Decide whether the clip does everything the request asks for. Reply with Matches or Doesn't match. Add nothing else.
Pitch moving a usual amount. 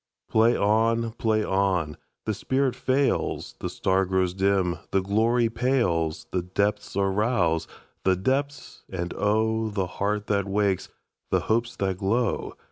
Matches